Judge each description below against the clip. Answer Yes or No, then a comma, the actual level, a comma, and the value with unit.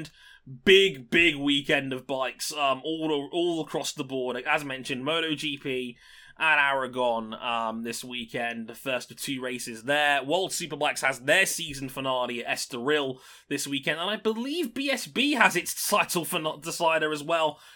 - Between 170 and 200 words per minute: No, average, 160 wpm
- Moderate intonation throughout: Yes, average, 4.1 semitones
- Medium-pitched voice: Yes, medium, 145 Hz